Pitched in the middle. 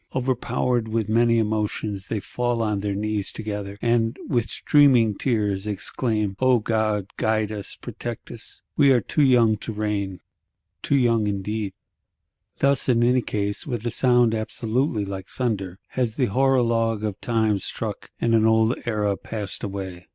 No: low, 110 Hz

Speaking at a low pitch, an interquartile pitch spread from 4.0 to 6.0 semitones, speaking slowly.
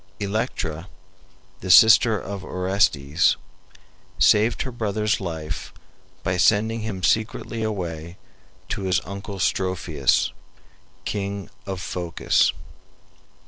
No: very low, 95 Hz; average, 3.4 semitones; slow, 95 wpm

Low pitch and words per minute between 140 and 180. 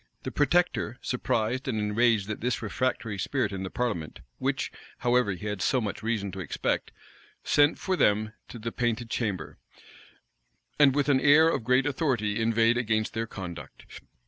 Yes: low, 115 Hz; average, 165 wpm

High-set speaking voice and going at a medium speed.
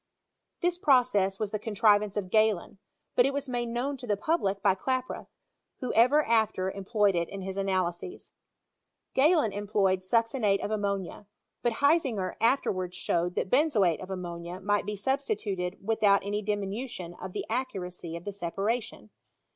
Yes: high, 205 Hz; average, 155 wpm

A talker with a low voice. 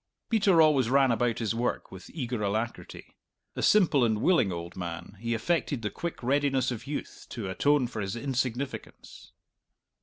Yes: low, 120 Hz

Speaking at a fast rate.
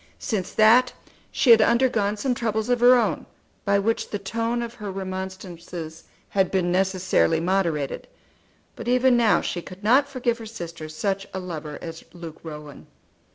No: average, 160 wpm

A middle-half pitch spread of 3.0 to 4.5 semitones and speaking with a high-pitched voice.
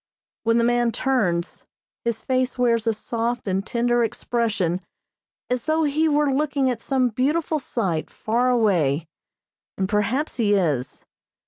Yes: average, 3.9 semitones; high, 235 Hz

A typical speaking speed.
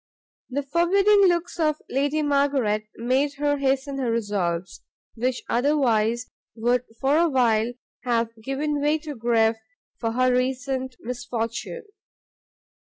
No: slow, 120 wpm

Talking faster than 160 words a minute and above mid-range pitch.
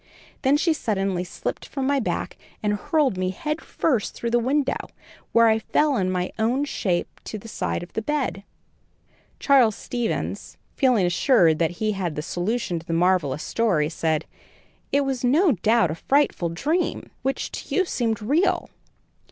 Yes: average, 170 wpm; high, 225 Hz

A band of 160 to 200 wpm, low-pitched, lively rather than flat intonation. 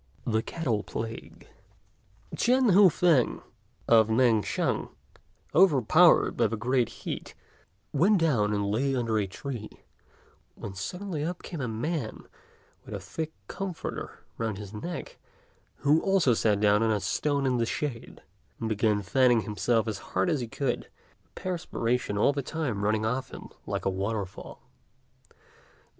No: average, 150 wpm; low, 120 Hz; wide, 6.0 semitones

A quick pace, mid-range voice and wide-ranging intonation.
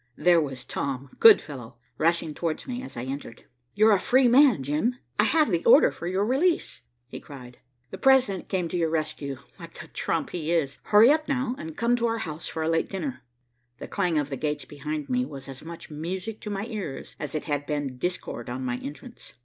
Yes: fast, 215 wpm; medium, 165 Hz; wide, 7.2 semitones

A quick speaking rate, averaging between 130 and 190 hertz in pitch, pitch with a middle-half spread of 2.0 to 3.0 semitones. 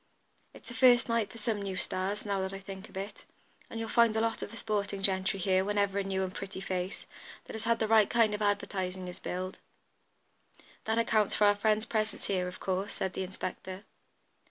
No: fast, 215 wpm; high, 200 Hz; narrow, 2.4 semitones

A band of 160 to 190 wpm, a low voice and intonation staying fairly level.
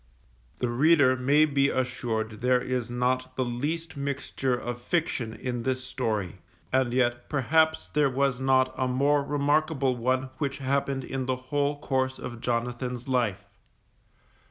No: average, 145 wpm; low, 130 Hz; narrow, 2.2 semitones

